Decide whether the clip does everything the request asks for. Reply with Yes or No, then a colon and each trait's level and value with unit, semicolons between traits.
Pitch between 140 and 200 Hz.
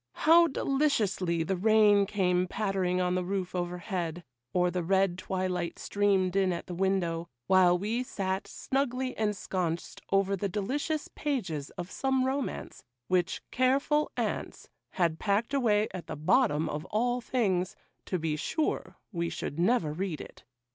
Yes: high, 190 Hz